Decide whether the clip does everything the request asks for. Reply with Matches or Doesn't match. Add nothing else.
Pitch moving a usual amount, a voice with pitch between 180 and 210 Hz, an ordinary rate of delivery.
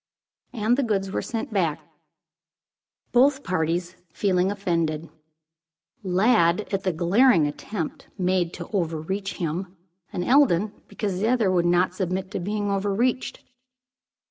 Doesn't match